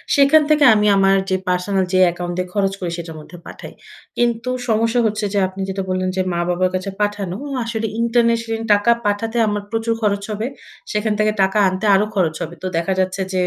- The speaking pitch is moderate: No, high, 205 Hz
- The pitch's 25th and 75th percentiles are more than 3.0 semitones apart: Yes, average, 3.4 semitones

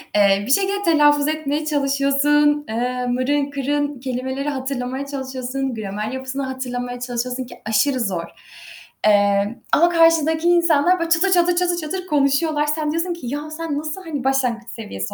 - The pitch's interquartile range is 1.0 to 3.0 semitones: No, average, 3.8 semitones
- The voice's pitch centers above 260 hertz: Yes, very high, 280 Hz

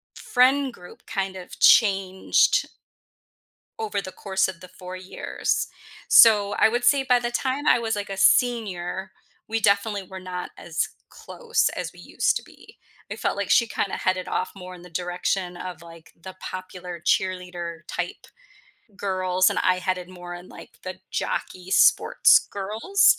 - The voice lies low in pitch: No, high, 190 Hz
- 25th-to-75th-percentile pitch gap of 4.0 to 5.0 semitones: No, average, 2.9 semitones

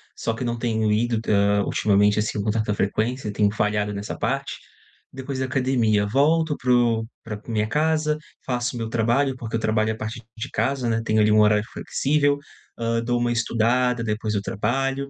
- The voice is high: No, low, 115 Hz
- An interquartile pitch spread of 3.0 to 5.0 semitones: Yes, average, 3.3 semitones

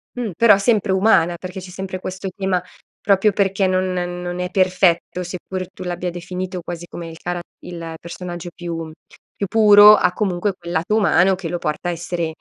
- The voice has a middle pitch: Yes, medium, 180 Hz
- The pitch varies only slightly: Yes, narrow, 1.7 semitones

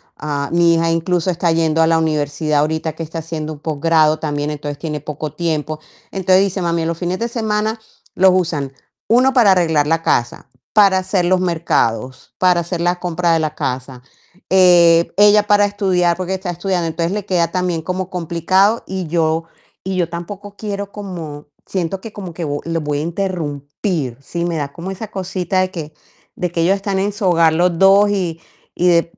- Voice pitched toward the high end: No, medium, 170 Hz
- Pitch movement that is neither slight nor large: Yes, average, 3.0 semitones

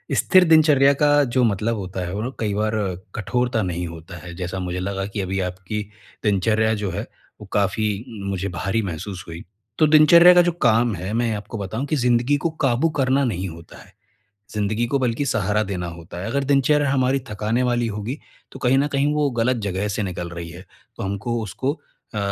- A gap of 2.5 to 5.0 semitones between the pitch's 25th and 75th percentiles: No, wide, 5.4 semitones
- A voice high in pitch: No, low, 110 Hz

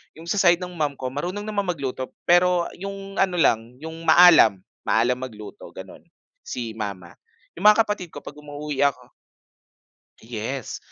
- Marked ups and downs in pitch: Yes, wide, 6.4 semitones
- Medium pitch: Yes, medium, 150 Hz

